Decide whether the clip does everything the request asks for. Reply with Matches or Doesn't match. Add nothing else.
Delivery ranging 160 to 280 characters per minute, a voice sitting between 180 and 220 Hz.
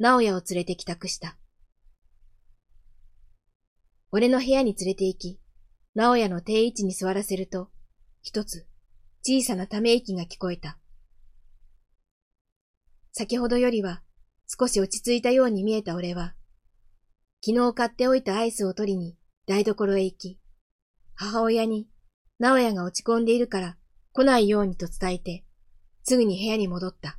Matches